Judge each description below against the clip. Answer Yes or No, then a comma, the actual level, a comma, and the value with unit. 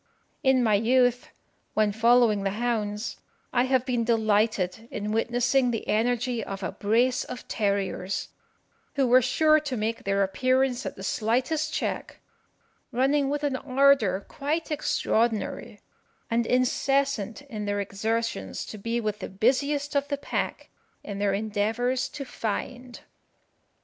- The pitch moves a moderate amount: Yes, average, 3.6 semitones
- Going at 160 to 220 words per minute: No, average, 140 wpm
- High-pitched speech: Yes, high, 235 Hz